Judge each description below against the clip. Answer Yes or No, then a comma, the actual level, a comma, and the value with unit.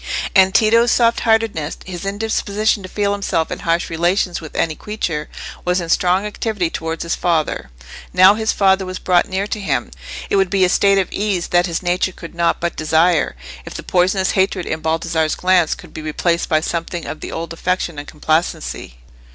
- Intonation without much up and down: No, average, 3.1 semitones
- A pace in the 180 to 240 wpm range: Yes, average, 190 wpm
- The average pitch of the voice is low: No, medium, 180 Hz